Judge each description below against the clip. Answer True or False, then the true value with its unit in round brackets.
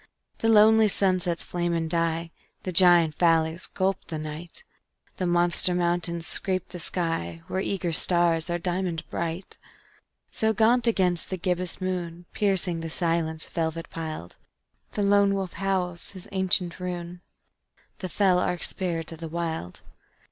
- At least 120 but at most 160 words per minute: True (145 wpm)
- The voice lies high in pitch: False (175 Hz)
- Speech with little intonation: True (2.1 semitones)